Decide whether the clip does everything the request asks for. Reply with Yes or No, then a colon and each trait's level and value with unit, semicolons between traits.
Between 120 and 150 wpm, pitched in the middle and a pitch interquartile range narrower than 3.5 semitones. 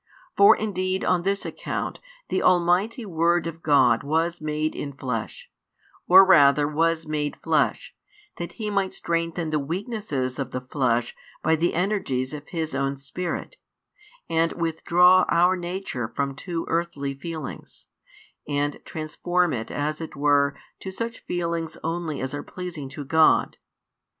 No: average, 145 wpm; medium, 165 Hz; average, 3.9 semitones